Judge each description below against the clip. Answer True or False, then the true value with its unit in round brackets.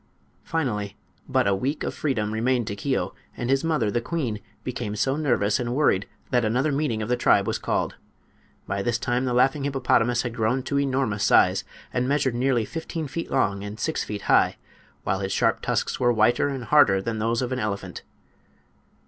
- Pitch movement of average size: True (4.0 semitones)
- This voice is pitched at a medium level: False (120 Hz)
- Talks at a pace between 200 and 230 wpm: False (190 wpm)